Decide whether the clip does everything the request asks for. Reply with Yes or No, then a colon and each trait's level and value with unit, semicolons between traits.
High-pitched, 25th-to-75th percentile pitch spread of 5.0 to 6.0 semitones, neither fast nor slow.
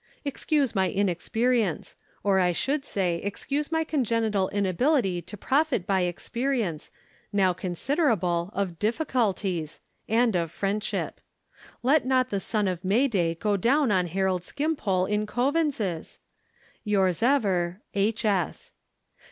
No: high, 205 Hz; wide, 5.6 semitones; slow, 115 wpm